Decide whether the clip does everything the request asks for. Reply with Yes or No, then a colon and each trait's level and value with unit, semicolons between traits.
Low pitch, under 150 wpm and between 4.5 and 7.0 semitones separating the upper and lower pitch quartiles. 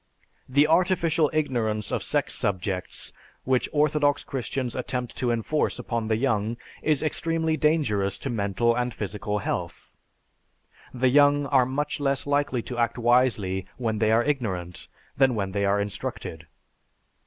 Yes: low, 125 Hz; average, 140 wpm; average, 5.1 semitones